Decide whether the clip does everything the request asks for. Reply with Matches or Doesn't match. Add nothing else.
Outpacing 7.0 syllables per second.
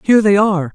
Matches